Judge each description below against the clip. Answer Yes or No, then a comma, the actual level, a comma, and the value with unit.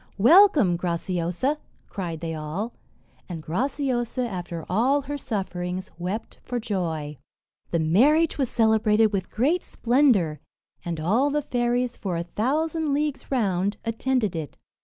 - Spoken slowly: Yes, slow, 130 wpm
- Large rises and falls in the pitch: Yes, wide, 7.0 semitones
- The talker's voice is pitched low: No, high, 215 Hz